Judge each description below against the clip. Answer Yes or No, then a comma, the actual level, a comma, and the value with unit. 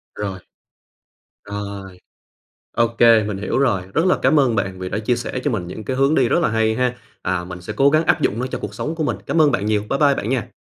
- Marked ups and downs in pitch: No, average, 4.9 semitones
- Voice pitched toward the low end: Yes, low, 110 Hz